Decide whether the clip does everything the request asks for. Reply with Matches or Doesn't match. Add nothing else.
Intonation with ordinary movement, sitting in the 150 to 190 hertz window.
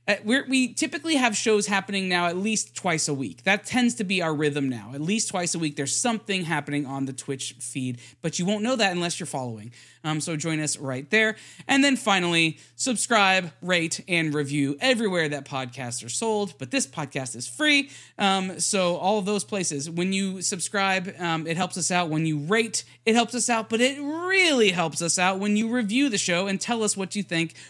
Doesn't match